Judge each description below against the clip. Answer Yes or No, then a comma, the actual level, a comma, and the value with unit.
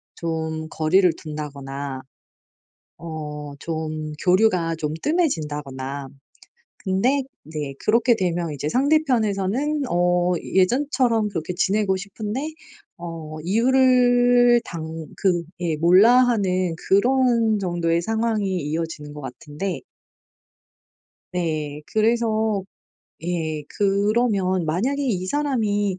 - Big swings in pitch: Yes, wide, 6.3 semitones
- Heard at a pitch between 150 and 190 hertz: Yes, medium, 185 Hz